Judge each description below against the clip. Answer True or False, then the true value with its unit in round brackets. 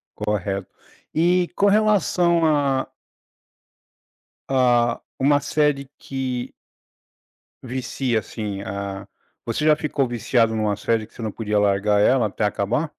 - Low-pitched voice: True (120 Hz)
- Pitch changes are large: True (5.7 semitones)